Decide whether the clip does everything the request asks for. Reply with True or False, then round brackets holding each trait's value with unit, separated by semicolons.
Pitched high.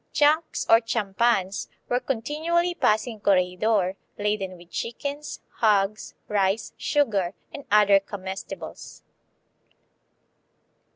True (215 Hz)